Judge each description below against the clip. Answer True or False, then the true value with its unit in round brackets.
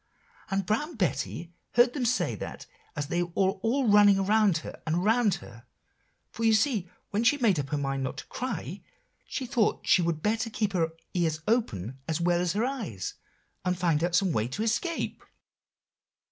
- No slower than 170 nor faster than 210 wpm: True (180 wpm)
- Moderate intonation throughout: False (5.7 semitones)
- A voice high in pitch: True (195 Hz)